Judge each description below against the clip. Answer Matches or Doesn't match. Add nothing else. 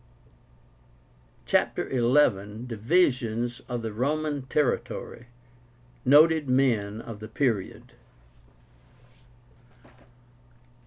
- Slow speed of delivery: Matches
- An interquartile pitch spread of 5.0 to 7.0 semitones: Doesn't match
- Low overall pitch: Matches